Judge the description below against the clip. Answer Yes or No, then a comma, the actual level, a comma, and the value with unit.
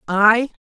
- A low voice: No, high, 220 Hz